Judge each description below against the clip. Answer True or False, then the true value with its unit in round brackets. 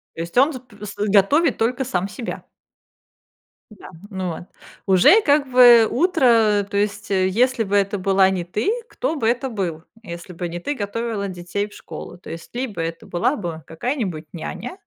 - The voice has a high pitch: True (205 Hz)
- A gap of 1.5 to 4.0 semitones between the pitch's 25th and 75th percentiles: False (5.2 semitones)